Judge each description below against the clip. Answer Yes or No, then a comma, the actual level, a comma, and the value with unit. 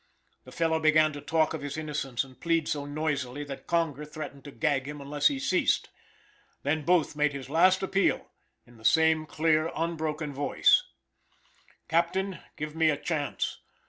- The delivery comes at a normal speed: Yes, average, 165 wpm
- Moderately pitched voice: Yes, medium, 155 Hz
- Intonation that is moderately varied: No, narrow, 2.2 semitones